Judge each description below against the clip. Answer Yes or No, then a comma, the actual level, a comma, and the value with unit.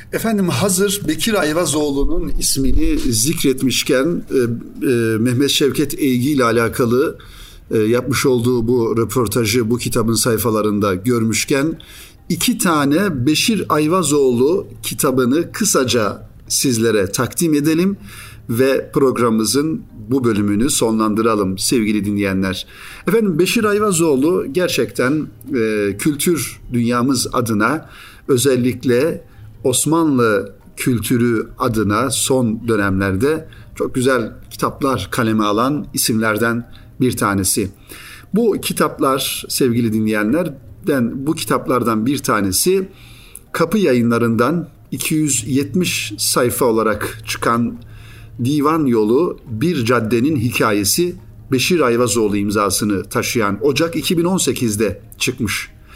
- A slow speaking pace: Yes, slow, 90 wpm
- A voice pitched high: No, low, 120 Hz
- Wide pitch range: No, average, 4.8 semitones